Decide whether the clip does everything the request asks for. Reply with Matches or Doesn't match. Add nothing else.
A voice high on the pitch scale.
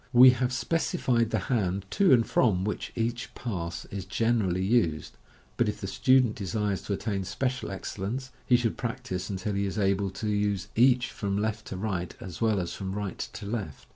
Doesn't match